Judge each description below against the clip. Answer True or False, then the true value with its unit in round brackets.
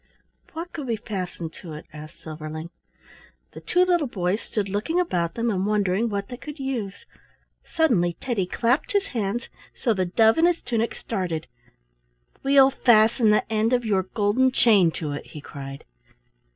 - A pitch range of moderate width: False (5.7 semitones)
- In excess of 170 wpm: False (165 wpm)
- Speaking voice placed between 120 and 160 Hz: False (215 Hz)